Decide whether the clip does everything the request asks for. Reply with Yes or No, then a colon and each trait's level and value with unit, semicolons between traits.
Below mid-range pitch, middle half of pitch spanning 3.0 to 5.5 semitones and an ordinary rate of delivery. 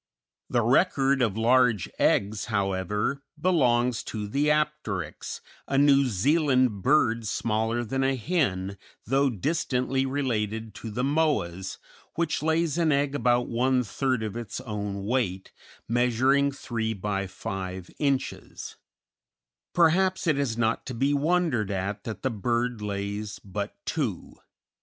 No: low, 120 Hz; average, 5.0 semitones; slow, 130 wpm